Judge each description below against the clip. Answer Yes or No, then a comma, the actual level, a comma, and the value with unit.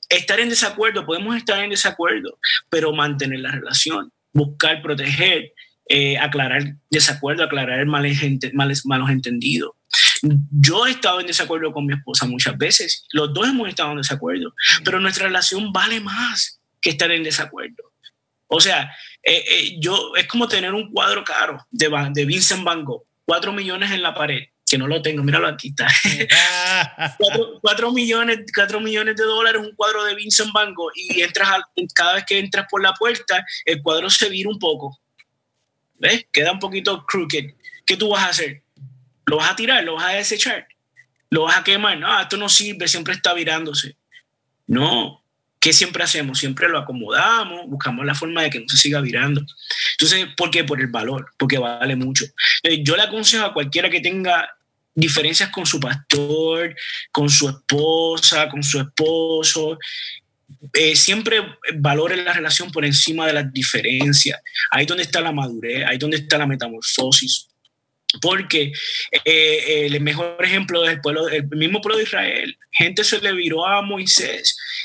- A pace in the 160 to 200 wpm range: Yes, average, 170 wpm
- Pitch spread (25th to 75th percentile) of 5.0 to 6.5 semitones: Yes, wide, 5.5 semitones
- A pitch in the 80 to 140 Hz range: No, medium, 160 Hz